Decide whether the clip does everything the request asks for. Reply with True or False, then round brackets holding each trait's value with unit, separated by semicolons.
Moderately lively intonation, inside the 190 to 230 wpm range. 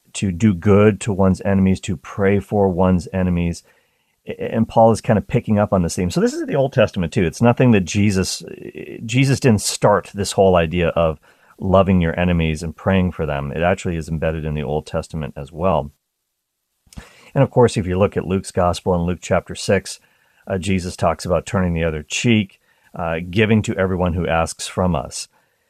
True (3.9 semitones; 200 wpm)